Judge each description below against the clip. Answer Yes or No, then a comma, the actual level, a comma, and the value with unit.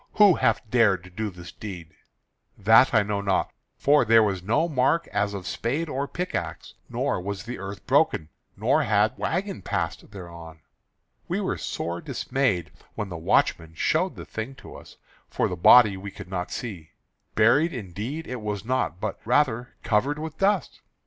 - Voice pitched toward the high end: No, low, 105 Hz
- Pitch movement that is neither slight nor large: No, wide, 5.7 semitones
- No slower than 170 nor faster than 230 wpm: Yes, average, 175 wpm